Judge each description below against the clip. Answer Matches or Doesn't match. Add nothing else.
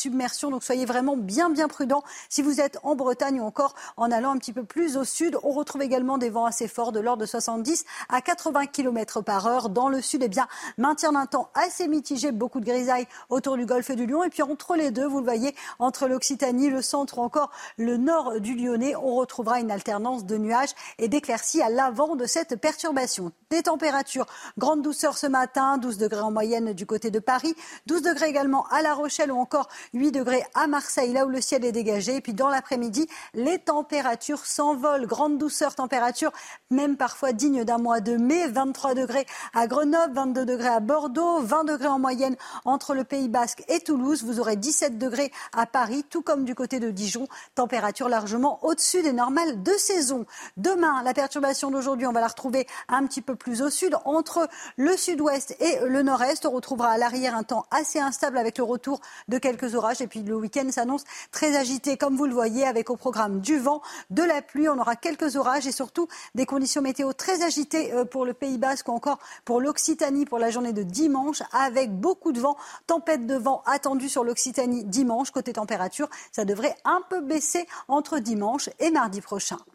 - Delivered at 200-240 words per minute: Matches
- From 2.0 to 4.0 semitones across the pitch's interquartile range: Matches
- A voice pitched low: Doesn't match